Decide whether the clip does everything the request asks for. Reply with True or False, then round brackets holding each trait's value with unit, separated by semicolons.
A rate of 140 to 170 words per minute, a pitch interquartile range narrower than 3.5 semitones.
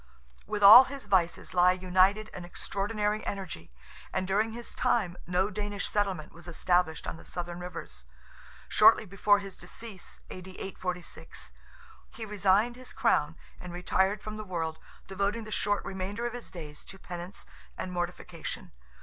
True (150 wpm; 2.8 semitones)